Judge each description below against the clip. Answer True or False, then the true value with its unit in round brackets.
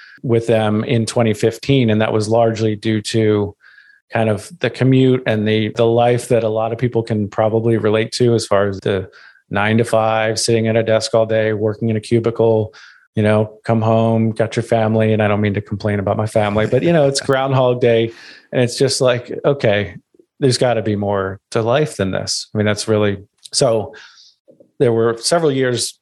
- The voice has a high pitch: False (115 Hz)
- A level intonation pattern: True (1.7 semitones)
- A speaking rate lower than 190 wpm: False (205 wpm)